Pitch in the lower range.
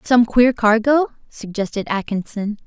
No: high, 220 Hz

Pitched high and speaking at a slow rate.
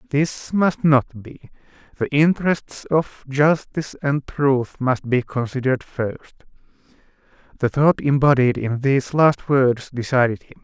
No: low, 135 Hz; slow, 130 wpm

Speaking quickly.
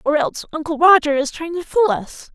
Yes: fast, 230 wpm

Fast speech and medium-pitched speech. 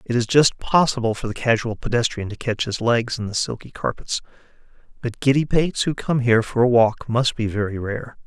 No: fast, 210 wpm; low, 120 Hz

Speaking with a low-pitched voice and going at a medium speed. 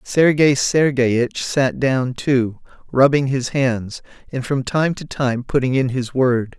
Yes: low, 130 Hz; average, 155 wpm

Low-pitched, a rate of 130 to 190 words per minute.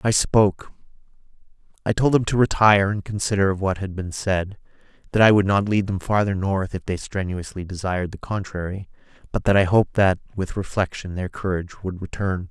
Yes: very low, 95 Hz; average, 185 wpm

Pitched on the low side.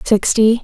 No: high, 220 Hz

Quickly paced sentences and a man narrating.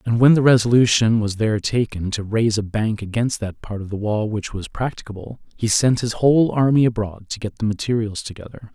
Yes: fast, 215 wpm; male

